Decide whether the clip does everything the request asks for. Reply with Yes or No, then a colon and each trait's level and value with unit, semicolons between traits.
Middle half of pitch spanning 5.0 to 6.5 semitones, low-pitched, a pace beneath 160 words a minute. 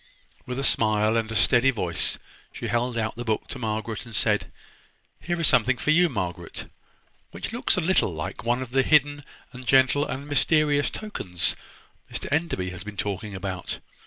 No: wide, 5.6 semitones; low, 120 Hz; average, 180 wpm